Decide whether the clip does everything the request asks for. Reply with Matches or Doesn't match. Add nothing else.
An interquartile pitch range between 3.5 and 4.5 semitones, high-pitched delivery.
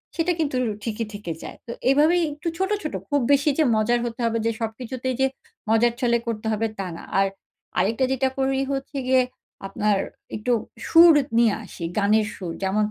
Matches